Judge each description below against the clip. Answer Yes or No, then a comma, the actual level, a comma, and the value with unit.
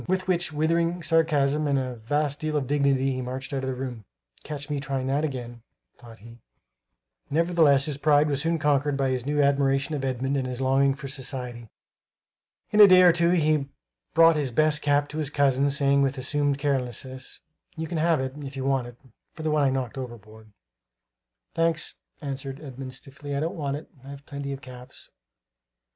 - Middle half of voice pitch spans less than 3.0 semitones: Yes, narrow, 2.5 semitones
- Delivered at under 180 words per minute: No, average, 190 wpm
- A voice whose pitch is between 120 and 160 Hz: Yes, medium, 140 Hz